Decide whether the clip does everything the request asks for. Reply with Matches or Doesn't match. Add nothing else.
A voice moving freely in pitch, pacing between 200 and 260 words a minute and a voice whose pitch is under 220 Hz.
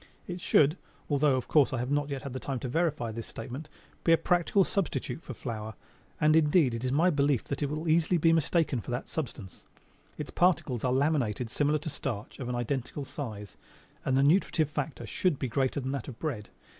Doesn't match